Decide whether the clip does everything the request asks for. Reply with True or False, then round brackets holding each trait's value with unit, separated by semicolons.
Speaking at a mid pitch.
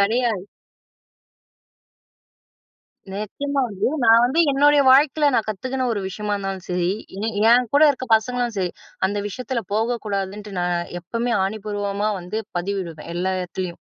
False (215 Hz)